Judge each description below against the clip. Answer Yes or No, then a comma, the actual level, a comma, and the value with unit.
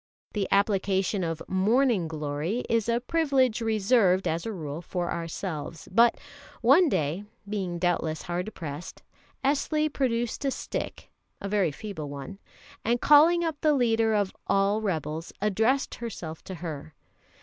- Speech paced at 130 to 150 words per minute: Yes, average, 140 wpm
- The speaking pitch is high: Yes, high, 200 Hz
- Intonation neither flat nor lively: No, wide, 6.0 semitones